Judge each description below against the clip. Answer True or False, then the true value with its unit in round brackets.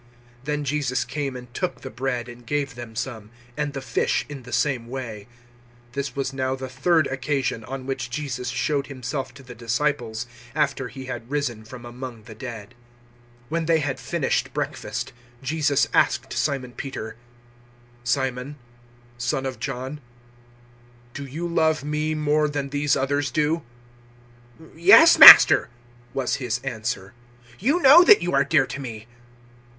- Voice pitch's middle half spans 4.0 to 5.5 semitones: False (3.3 semitones)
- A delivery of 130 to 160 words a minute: True (155 wpm)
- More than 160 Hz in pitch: False (135 Hz)